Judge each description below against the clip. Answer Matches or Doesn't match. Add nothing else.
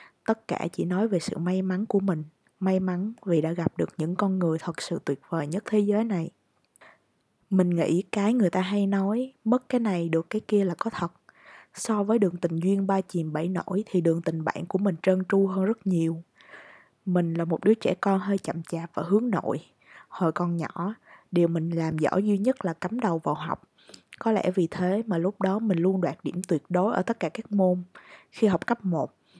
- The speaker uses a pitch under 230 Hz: Matches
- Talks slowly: Doesn't match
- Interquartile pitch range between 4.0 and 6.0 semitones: Doesn't match